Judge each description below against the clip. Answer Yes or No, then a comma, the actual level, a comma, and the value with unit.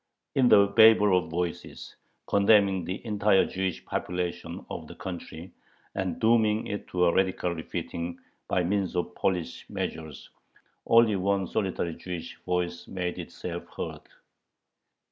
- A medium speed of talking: No, slow, 130 wpm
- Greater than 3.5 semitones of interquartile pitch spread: No, narrow, 2.6 semitones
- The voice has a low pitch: Yes, very low, 95 Hz